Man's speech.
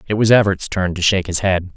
Yes: male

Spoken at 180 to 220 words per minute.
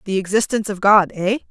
Yes: average, 200 wpm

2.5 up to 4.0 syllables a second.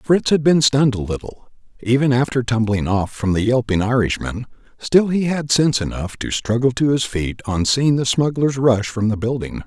No: 5.1 syllables/s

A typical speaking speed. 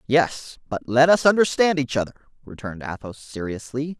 Yes: average, 150 wpm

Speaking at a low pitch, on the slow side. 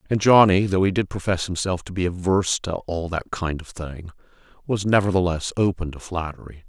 No: very low, 90 Hz; average, 190 wpm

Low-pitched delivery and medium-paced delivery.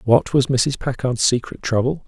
Yes: low, 125 Hz; average, 175 wpm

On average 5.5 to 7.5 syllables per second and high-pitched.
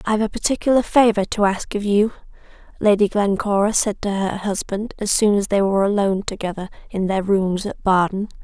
Yes: 5.6 syllables/s; high, 200 Hz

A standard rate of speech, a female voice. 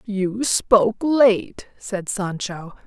No: slow, 105 wpm; female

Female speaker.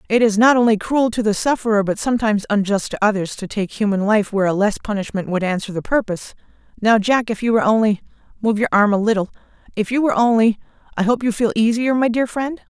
Yes: female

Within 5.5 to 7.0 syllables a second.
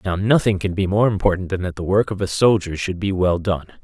Yes: 5.6 syllables/s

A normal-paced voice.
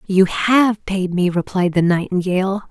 Yes: average, 155 wpm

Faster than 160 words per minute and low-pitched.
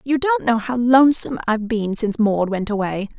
No: fast, 205 wpm; high, 235 Hz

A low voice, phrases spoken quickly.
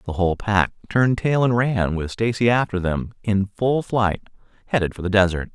No: low, 105 Hz; average, 195 wpm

